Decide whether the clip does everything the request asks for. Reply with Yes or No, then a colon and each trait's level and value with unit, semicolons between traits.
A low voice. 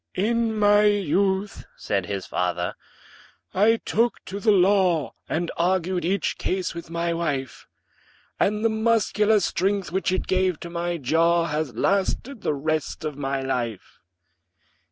No: medium, 180 Hz